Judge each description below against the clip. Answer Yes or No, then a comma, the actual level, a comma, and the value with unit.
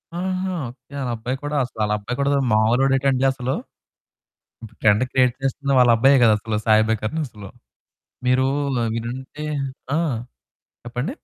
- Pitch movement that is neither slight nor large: Yes, average, 3.3 semitones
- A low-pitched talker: Yes, low, 125 Hz